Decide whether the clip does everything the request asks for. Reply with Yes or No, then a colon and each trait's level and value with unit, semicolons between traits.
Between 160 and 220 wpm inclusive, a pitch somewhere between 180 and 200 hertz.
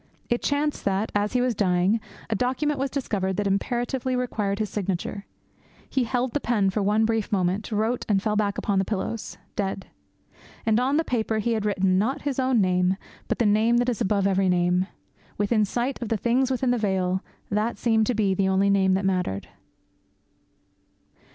No: average, 190 wpm; high, 210 Hz